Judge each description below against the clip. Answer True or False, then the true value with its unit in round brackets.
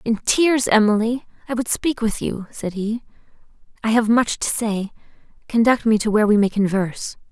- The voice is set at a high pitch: True (225 Hz)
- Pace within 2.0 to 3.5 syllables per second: False (5.1 syllables/s)